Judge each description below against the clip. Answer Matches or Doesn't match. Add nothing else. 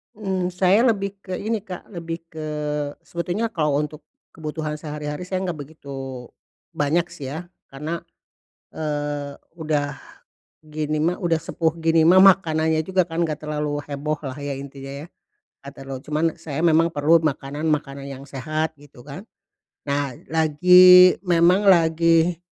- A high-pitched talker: Doesn't match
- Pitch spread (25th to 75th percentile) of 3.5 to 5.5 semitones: Doesn't match